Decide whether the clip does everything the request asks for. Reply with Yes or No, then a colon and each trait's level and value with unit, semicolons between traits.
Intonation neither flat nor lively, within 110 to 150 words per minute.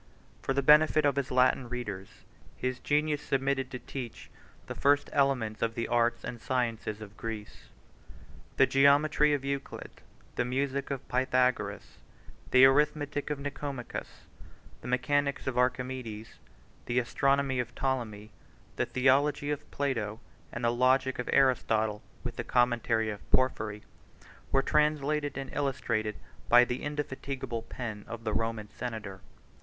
Yes: average, 3.2 semitones; average, 140 wpm